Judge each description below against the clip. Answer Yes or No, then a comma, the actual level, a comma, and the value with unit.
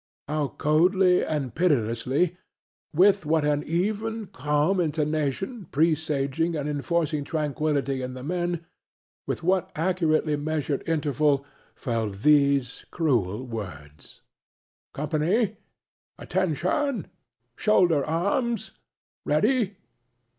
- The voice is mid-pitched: Yes, medium, 155 Hz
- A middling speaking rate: No, slow, 90 wpm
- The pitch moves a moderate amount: Yes, average, 4.3 semitones